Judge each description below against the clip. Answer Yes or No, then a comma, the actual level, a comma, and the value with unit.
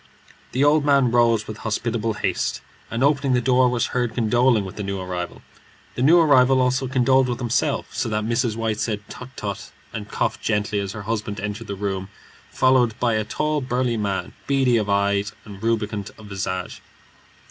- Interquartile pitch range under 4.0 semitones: Yes, average, 3.5 semitones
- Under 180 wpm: No, average, 185 wpm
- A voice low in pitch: Yes, low, 115 Hz